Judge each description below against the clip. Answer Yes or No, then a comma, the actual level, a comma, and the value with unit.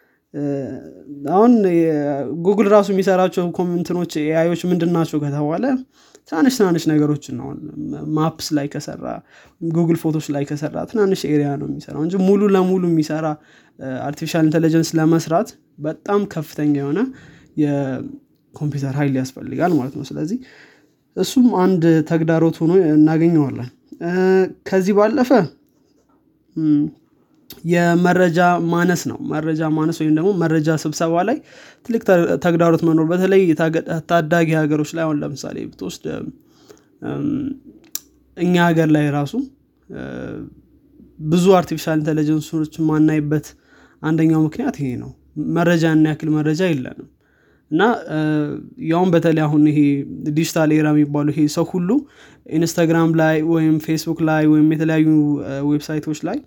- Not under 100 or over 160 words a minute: Yes, fast, 110 wpm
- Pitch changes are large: No, narrow, 2.5 semitones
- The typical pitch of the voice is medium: Yes, medium, 160 Hz